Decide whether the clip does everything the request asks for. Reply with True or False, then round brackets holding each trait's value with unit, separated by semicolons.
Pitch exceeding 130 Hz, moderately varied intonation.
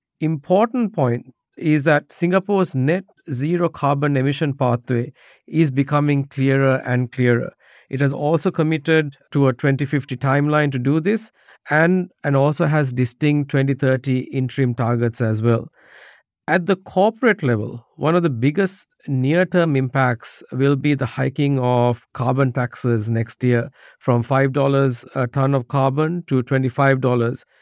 True (140 Hz; 3.4 semitones)